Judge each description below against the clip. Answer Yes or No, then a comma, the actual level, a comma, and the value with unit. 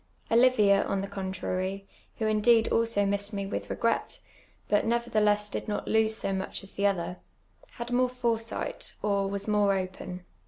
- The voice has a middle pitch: No, high, 205 Hz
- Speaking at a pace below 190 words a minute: Yes, average, 160 wpm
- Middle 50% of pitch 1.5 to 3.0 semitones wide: Yes, narrow, 2.4 semitones